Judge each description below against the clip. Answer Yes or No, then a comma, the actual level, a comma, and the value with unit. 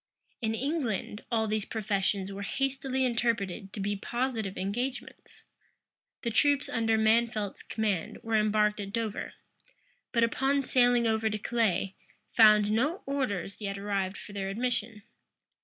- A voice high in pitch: Yes, high, 220 Hz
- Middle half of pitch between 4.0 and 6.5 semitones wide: No, average, 3.1 semitones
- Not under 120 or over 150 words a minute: Yes, slow, 135 wpm